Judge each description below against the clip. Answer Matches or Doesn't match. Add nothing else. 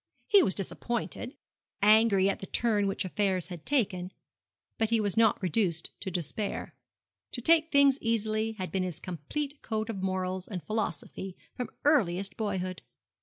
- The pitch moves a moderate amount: Matches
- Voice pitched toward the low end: Doesn't match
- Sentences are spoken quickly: Doesn't match